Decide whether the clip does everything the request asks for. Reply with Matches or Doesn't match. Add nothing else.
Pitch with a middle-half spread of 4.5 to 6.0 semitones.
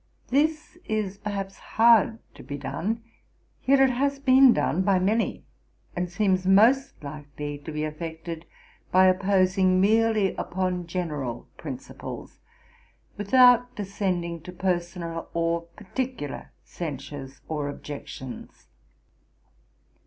Matches